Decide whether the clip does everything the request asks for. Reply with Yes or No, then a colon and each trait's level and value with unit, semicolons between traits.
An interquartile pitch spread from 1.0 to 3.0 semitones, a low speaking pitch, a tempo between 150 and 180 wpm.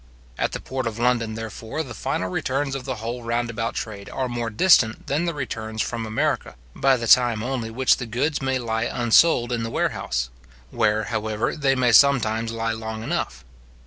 No: narrow, 2.6 semitones; low, 115 Hz; average, 190 wpm